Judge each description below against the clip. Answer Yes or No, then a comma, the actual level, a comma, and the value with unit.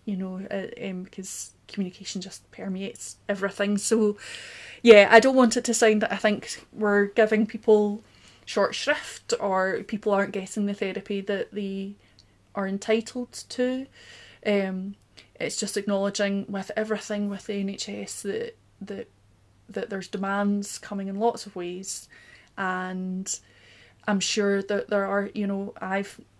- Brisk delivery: No, average, 145 wpm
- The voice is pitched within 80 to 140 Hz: No, high, 200 Hz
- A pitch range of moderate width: No, narrow, 1.7 semitones